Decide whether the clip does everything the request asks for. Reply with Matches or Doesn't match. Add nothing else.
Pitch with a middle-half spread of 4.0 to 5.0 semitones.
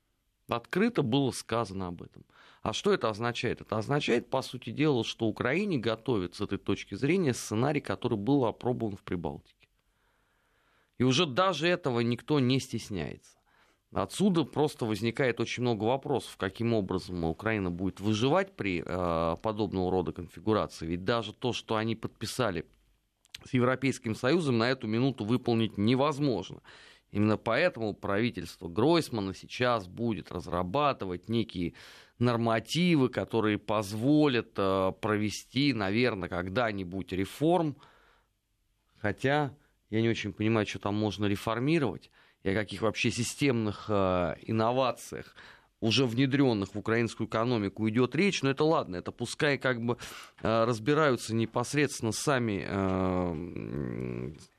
Matches